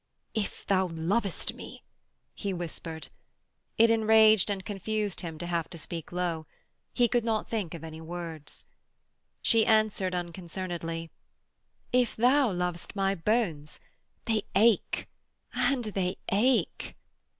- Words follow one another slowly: Yes, slow, 125 wpm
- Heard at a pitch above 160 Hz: Yes, high, 190 Hz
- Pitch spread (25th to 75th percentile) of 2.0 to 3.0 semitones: No, average, 4.5 semitones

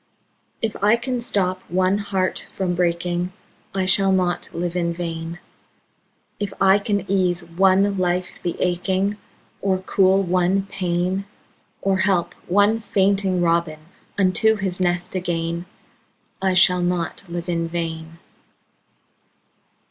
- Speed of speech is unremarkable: No, slow, 125 wpm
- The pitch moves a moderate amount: No, narrow, 2.0 semitones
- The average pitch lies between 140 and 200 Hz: Yes, medium, 185 Hz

